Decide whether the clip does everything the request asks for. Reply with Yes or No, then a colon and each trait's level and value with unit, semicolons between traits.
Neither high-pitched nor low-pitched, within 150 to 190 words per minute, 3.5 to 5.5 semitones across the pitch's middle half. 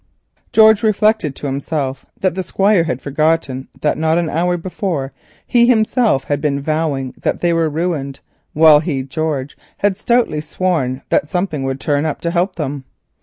Yes: medium, 160 Hz; average, 160 wpm; average, 4.5 semitones